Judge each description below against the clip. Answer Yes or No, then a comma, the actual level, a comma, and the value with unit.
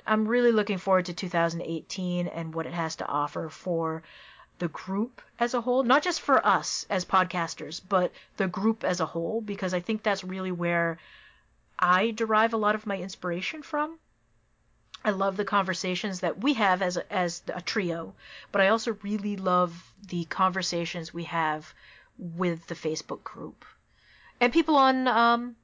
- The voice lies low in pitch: No, medium, 185 Hz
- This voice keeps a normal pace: Yes, average, 170 wpm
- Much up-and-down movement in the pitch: No, average, 3.9 semitones